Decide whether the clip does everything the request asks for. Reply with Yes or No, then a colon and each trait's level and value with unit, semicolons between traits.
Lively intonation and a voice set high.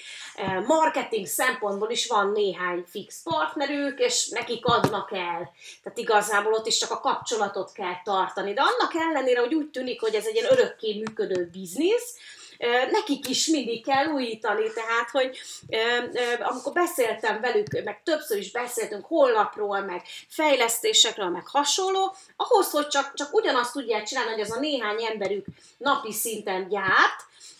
Yes: wide, 7.2 semitones; high, 245 Hz